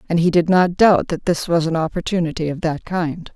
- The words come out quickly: Yes, fast, 235 wpm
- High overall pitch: No, medium, 170 Hz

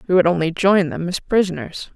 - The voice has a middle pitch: Yes, medium, 180 Hz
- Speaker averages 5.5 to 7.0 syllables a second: Yes, 5.6 syllables/s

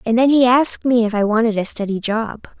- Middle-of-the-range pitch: No, high, 230 Hz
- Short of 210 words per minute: No, fast, 255 wpm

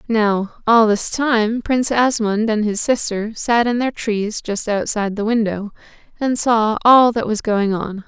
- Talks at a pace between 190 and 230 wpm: No, average, 180 wpm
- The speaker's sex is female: Yes, female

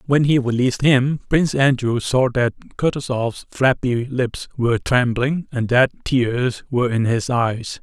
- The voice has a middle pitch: No, low, 125 Hz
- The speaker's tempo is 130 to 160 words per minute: Yes, average, 155 wpm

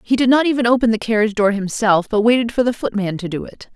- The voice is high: Yes, high, 220 Hz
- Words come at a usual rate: No, fast, 270 wpm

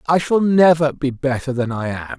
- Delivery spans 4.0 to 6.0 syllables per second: Yes, 5.0 syllables/s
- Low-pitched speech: No, medium, 145 Hz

